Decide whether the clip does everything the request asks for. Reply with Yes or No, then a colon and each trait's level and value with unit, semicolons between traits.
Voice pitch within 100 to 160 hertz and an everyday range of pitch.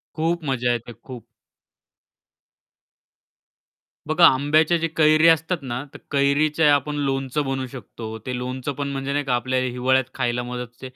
Yes: low, 135 Hz; average, 3.2 semitones